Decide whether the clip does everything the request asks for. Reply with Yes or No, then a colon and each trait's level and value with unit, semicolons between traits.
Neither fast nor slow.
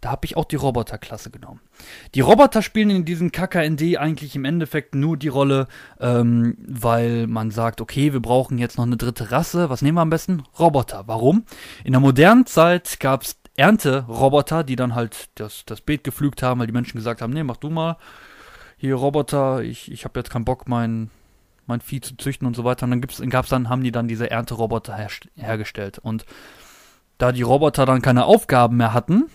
No: fast, 205 wpm